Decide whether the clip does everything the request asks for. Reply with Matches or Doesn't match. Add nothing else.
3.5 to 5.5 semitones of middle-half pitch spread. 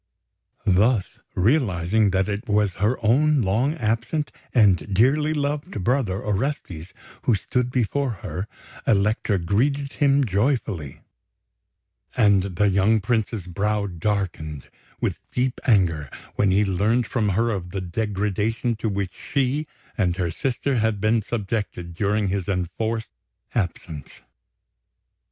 Matches